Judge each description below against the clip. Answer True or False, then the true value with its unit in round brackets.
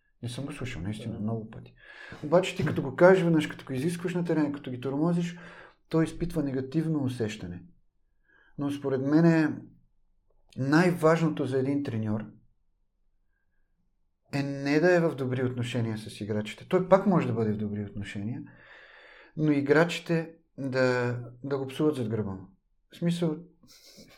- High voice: False (135 Hz)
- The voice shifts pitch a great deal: True (6.5 semitones)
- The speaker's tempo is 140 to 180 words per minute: True (150 wpm)